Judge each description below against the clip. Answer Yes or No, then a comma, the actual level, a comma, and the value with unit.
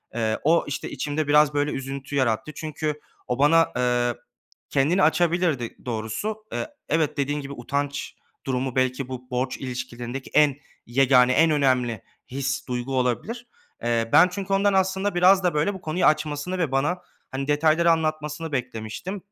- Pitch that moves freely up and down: No, average, 4.2 semitones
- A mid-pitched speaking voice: Yes, medium, 145 Hz